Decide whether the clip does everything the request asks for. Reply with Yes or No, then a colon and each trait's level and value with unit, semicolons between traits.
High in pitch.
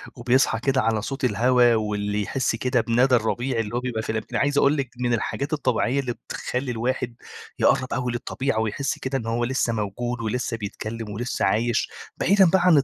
No: low, 120 Hz